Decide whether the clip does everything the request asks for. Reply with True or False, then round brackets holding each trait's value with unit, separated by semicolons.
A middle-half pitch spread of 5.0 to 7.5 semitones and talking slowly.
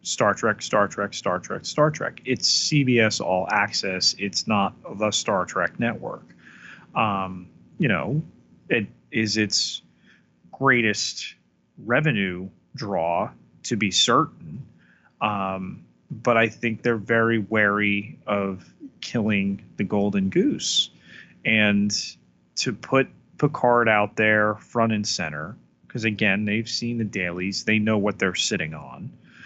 False (2.8 semitones; 130 wpm)